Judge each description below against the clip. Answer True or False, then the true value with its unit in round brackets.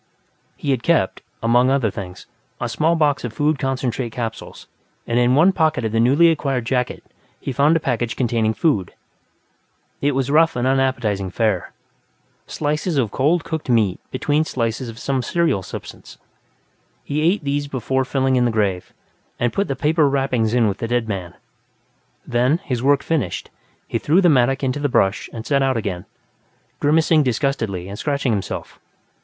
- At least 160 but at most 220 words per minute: True (170 wpm)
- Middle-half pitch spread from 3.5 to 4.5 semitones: True (4.2 semitones)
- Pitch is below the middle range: True (130 Hz)